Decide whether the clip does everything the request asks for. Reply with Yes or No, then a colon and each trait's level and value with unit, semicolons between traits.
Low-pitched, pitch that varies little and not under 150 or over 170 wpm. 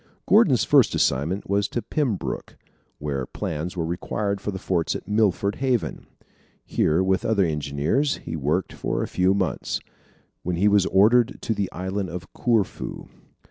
No: very low, 95 Hz; average, 3.6 semitones; average, 155 wpm